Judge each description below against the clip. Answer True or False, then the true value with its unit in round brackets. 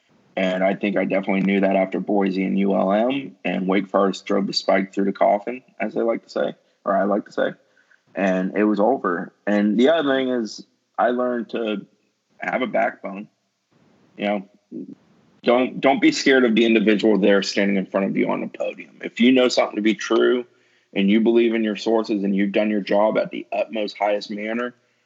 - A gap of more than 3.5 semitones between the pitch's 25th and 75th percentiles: False (2.9 semitones)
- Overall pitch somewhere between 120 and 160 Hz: False (105 Hz)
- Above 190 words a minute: True (205 wpm)